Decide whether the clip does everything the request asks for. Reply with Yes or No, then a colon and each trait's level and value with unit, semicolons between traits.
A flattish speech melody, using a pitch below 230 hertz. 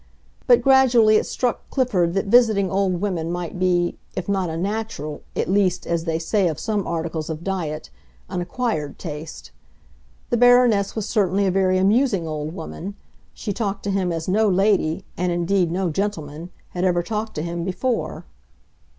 No: average, 3.6 semitones; medium, 185 Hz